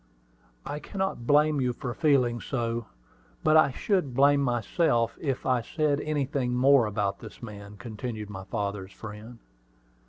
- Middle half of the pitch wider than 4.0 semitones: Yes, average, 4.7 semitones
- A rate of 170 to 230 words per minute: No, average, 145 wpm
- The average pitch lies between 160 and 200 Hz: No, low, 125 Hz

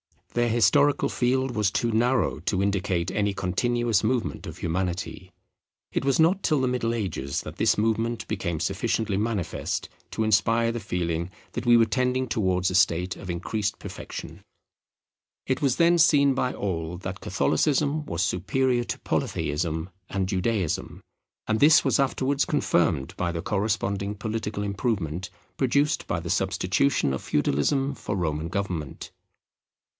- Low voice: Yes, low, 105 Hz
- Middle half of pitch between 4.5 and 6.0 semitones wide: Yes, wide, 5.5 semitones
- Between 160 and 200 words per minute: No, average, 145 wpm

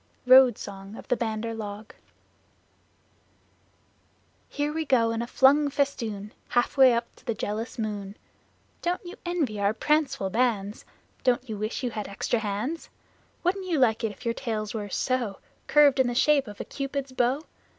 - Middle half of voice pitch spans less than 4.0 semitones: No, average, 4.3 semitones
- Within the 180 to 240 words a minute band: No, average, 165 wpm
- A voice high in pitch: Yes, high, 240 Hz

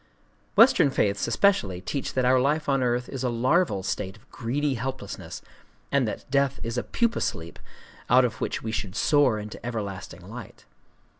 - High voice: No, low, 125 Hz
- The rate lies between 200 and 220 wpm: No, average, 170 wpm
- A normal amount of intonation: Yes, average, 4.4 semitones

